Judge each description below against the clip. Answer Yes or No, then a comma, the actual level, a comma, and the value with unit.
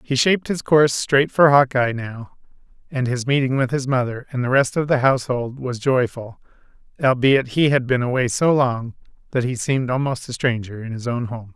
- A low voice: Yes, low, 130 Hz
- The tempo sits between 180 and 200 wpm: Yes, average, 195 wpm